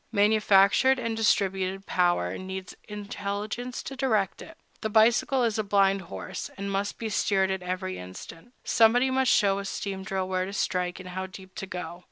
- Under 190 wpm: Yes, average, 180 wpm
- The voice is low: No, high, 195 Hz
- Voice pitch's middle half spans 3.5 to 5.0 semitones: No, narrow, 2.6 semitones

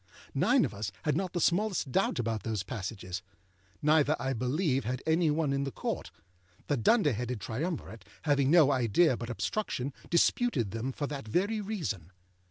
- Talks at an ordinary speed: Yes, average, 170 wpm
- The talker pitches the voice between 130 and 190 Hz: Yes, low, 135 Hz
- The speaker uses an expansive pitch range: Yes, wide, 6.0 semitones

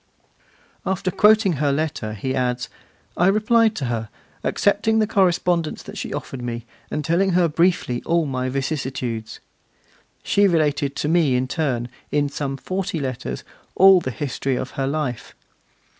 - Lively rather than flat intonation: Yes, wide, 5.9 semitones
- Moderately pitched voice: Yes, medium, 150 Hz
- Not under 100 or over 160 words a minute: Yes, average, 150 wpm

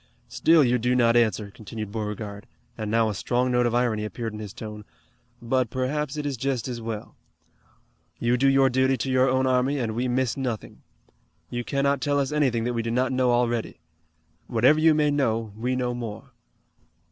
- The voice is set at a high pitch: No, low, 125 Hz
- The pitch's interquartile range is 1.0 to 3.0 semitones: Yes, narrow, 2.6 semitones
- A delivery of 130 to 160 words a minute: No, average, 195 wpm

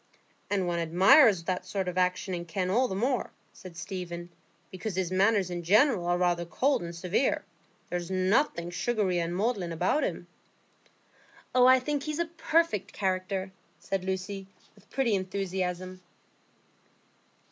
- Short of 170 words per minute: Yes, average, 145 wpm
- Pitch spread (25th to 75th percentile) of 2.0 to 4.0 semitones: Yes, average, 3.5 semitones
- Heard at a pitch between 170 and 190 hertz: Yes, medium, 185 Hz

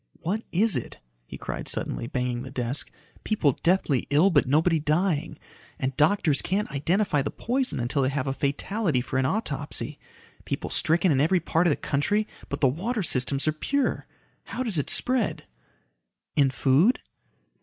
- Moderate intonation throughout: No, wide, 6.2 semitones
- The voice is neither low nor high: Yes, medium, 155 Hz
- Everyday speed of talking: Yes, average, 165 wpm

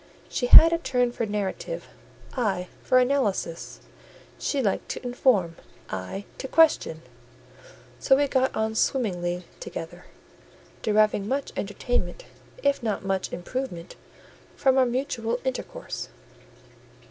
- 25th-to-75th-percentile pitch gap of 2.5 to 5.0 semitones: No, wide, 5.4 semitones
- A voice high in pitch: Yes, high, 235 Hz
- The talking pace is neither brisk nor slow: No, slow, 115 wpm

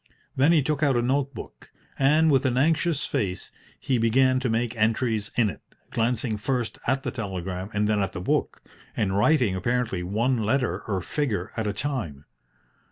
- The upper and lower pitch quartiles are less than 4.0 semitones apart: No, average, 4.5 semitones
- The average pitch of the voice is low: Yes, low, 115 Hz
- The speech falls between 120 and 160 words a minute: No, average, 180 wpm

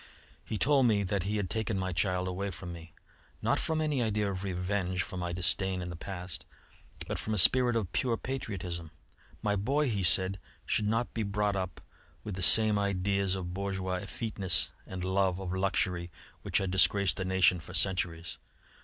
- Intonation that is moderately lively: No, narrow, 2.3 semitones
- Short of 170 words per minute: No, average, 185 wpm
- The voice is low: Yes, very low, 95 Hz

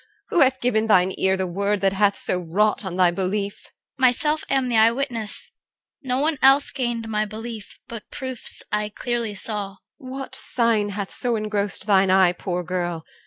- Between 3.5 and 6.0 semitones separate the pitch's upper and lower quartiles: Yes, average, 4.3 semitones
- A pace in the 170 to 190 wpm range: Yes, average, 180 wpm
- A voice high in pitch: Yes, high, 215 Hz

